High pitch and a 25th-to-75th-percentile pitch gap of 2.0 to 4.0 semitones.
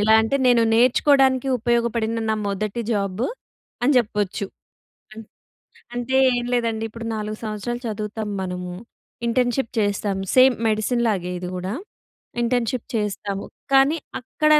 Yes: high, 225 Hz; average, 2.8 semitones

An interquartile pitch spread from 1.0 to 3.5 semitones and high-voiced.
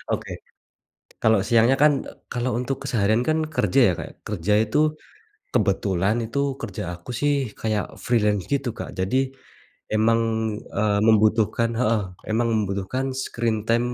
No: narrow, 2.6 semitones; low, 110 Hz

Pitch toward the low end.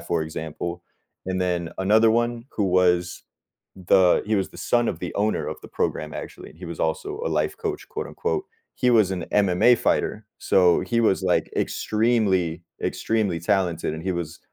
Yes: very low, 95 Hz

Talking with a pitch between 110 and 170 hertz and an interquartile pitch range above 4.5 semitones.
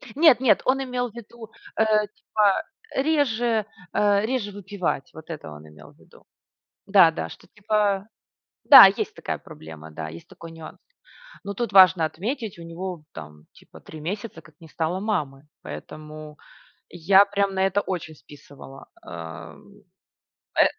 No: high, 190 Hz; wide, 5.6 semitones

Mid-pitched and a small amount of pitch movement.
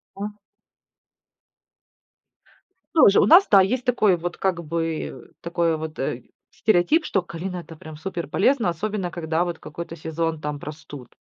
No: medium, 170 Hz; average, 3.4 semitones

